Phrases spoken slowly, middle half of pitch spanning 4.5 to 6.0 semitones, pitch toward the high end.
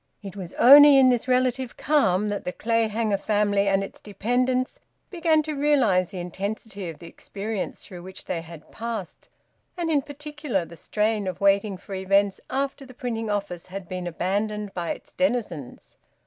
No: average, 170 wpm; average, 5.2 semitones; high, 210 Hz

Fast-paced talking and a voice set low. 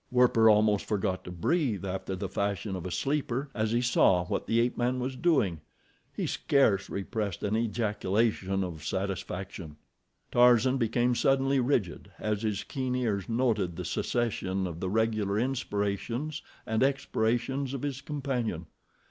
No: average, 145 wpm; low, 110 Hz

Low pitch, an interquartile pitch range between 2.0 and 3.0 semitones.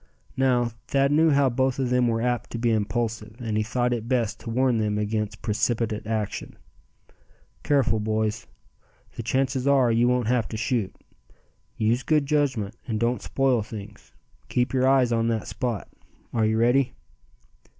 Yes: low, 120 Hz; average, 2.7 semitones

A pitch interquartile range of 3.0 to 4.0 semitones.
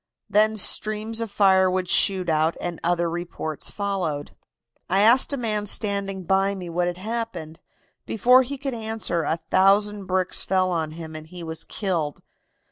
Yes: average, 3.6 semitones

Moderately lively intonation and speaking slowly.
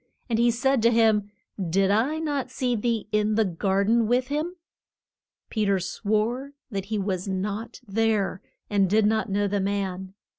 No: average, 3.1 semitones; average, 175 wpm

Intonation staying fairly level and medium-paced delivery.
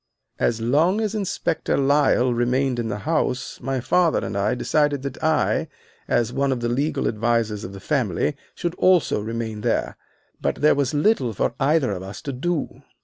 No: average, 4.5 semitones; average, 170 wpm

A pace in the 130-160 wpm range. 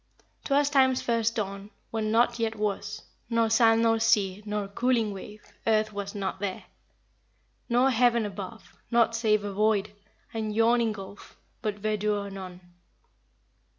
Yes: average, 140 wpm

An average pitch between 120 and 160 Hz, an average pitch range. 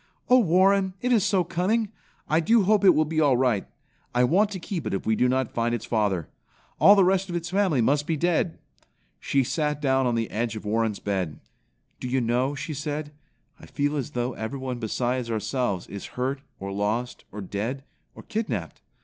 No: low, 135 Hz; wide, 7.0 semitones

